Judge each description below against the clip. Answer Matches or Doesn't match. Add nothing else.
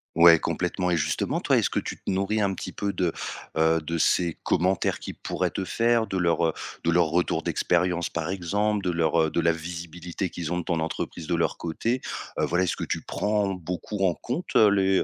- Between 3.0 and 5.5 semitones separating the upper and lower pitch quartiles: Doesn't match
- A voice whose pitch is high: Doesn't match